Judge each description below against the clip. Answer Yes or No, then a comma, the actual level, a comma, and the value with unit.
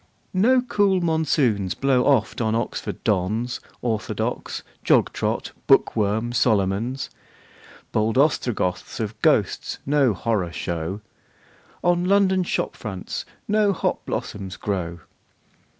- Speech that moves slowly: Yes, slow, 110 wpm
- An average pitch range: No, wide, 7.9 semitones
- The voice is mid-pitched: No, low, 115 Hz